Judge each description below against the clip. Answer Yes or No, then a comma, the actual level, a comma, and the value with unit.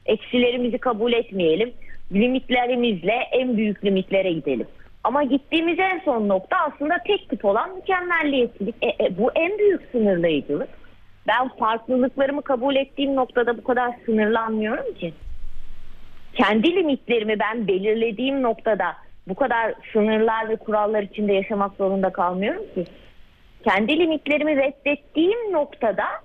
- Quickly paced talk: No, average, 120 wpm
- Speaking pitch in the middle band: No, high, 235 Hz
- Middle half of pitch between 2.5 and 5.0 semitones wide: No, wide, 5.4 semitones